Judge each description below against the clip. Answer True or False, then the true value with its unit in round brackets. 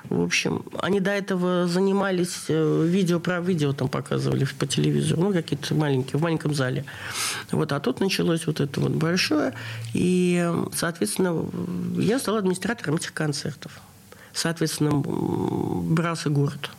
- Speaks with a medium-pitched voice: True (165 Hz)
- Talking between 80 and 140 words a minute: True (130 wpm)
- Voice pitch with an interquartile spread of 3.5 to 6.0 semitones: True (3.9 semitones)